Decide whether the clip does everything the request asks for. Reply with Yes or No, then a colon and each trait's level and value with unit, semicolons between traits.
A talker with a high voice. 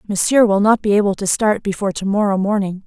Yes: high, 200 Hz